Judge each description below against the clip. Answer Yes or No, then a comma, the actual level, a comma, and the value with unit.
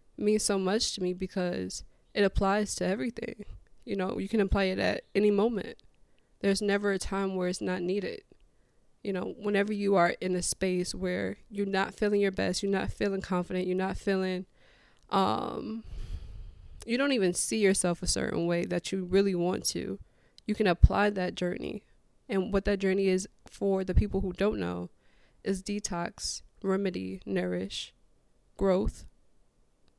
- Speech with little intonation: Yes, narrow, 2.0 semitones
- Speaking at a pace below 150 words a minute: No, average, 165 wpm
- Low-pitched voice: No, high, 190 Hz